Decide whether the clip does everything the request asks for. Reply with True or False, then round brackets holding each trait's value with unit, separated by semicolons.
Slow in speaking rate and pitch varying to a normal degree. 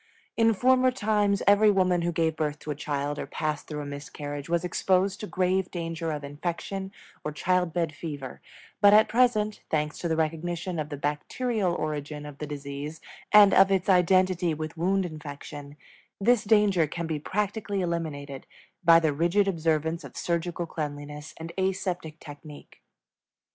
False (165 wpm; 4.2 semitones)